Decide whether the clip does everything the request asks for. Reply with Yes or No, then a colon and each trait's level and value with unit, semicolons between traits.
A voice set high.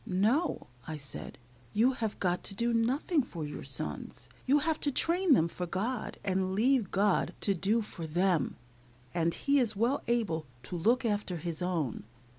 Yes: high, 205 Hz